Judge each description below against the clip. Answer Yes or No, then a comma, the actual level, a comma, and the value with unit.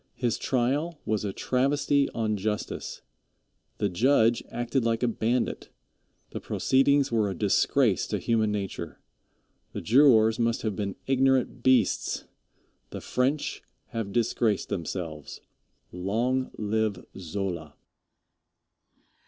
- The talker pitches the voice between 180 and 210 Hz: No, low, 115 Hz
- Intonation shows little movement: No, average, 4.0 semitones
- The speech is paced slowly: Yes, slow, 110 wpm